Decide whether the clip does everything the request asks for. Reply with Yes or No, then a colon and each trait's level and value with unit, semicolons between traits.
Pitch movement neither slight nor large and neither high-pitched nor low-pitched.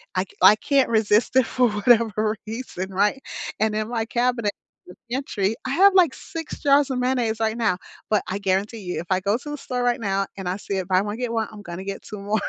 No: average, 3.9 semitones; high, 220 Hz